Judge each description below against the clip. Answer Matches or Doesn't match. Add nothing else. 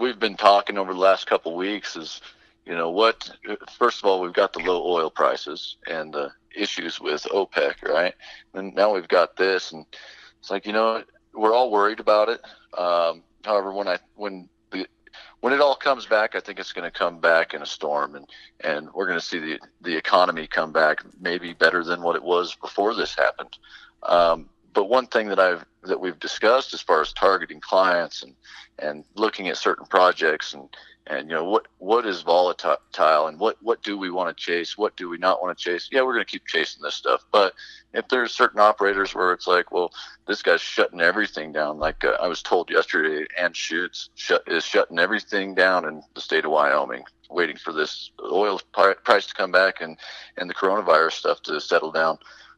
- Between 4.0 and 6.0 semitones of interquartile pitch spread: Matches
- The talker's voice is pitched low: Matches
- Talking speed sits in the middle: Doesn't match